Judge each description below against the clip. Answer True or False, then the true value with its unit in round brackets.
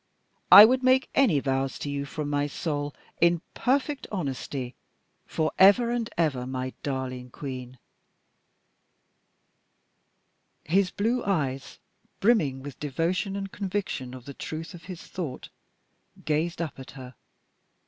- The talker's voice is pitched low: False (155 Hz)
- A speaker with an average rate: False (130 wpm)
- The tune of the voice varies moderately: False (6.6 semitones)